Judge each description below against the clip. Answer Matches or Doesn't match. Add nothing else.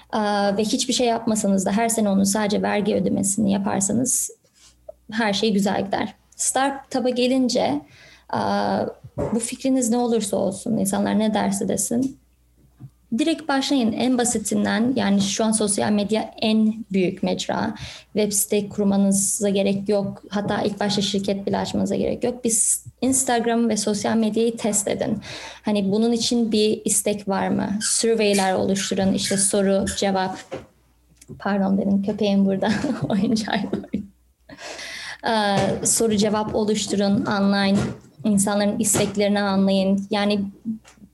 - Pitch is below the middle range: Doesn't match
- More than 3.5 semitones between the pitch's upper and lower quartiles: Doesn't match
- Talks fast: Doesn't match